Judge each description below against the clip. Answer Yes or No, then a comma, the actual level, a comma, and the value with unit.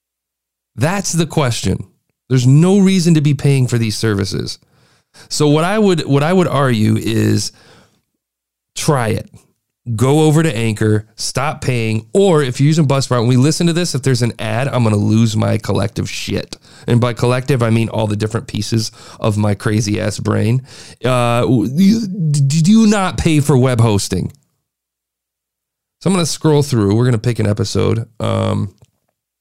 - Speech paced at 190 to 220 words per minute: No, average, 175 wpm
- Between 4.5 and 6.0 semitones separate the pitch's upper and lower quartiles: Yes, wide, 5.5 semitones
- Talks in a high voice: No, low, 120 Hz